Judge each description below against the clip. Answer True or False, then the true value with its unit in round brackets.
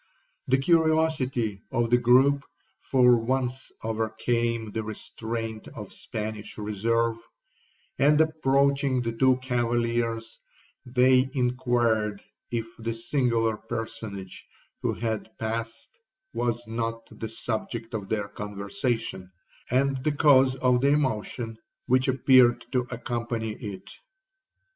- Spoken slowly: True (110 wpm)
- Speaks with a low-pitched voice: True (120 Hz)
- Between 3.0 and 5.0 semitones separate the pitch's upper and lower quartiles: False (2.6 semitones)